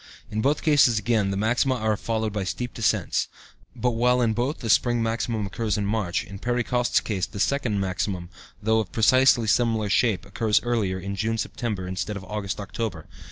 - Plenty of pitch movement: No, average, 3.2 semitones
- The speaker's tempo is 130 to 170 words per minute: No, average, 190 wpm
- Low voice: Yes, low, 110 Hz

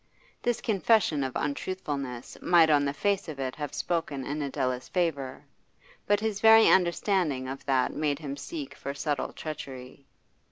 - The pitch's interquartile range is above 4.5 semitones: Yes, average, 5.3 semitones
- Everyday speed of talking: Yes, average, 155 wpm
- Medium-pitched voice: Yes, medium, 150 Hz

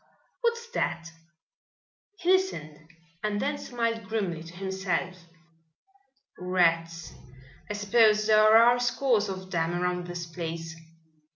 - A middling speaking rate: No, slow, 110 wpm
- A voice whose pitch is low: No, high, 190 Hz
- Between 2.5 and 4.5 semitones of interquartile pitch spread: No, average, 4.9 semitones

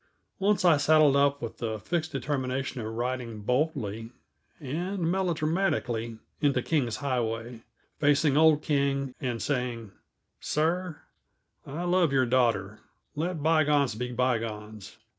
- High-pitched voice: No, low, 135 Hz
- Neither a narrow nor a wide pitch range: Yes, average, 4.9 semitones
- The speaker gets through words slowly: Yes, slow, 120 wpm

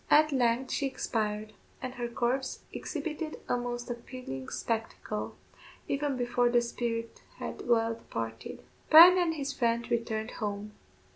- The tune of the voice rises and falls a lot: No, average, 3.0 semitones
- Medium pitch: No, high, 240 Hz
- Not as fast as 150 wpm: Yes, slow, 135 wpm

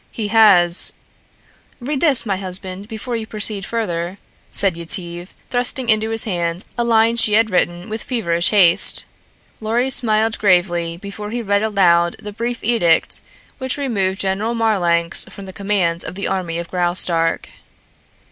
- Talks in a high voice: Yes, high, 200 Hz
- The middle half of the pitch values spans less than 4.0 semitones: No, average, 4.3 semitones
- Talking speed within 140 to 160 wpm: Yes, average, 155 wpm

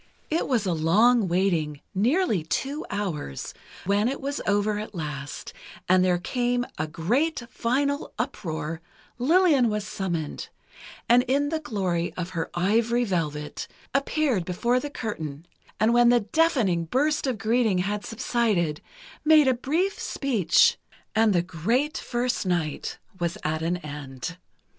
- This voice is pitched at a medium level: No, high, 210 Hz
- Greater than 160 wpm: No, average, 140 wpm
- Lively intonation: Yes, wide, 6.6 semitones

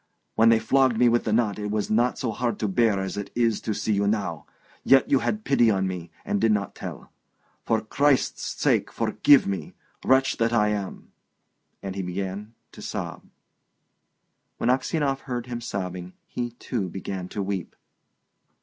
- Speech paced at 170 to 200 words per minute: Yes, average, 175 wpm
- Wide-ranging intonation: No, average, 3.5 semitones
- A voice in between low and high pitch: No, low, 110 Hz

